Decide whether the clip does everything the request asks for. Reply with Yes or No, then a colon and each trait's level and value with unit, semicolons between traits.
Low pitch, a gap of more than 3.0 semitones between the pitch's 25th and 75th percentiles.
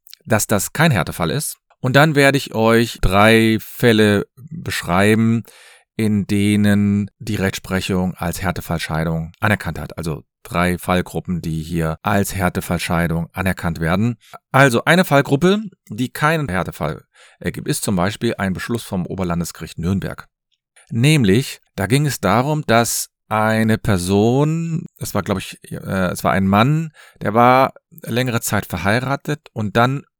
Yes: low, 110 Hz; wide, 5.6 semitones